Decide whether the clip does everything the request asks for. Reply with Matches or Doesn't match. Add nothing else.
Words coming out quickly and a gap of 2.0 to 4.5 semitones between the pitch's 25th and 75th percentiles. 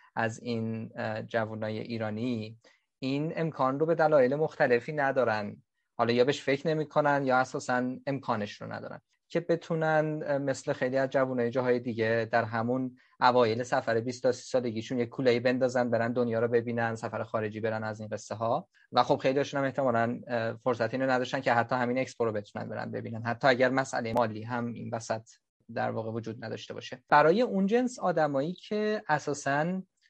Matches